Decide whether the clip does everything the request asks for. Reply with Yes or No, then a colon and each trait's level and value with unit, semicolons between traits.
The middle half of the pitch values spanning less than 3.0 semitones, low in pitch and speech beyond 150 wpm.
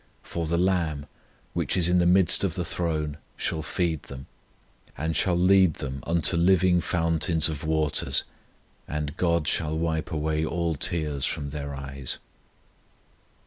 No: narrow, 2.5 semitones; very low, 80 Hz; average, 145 wpm